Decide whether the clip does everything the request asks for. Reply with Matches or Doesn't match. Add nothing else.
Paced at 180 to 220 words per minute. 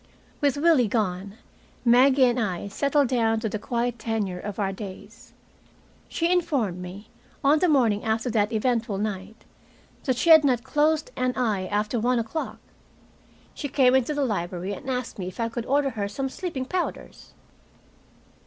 Doesn't match